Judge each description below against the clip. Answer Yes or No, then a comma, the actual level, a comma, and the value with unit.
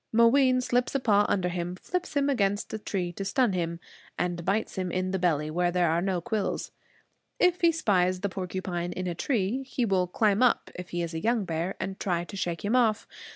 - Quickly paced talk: Yes, fast, 220 wpm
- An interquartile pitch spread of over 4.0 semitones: Yes, average, 4.5 semitones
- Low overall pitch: No, high, 190 Hz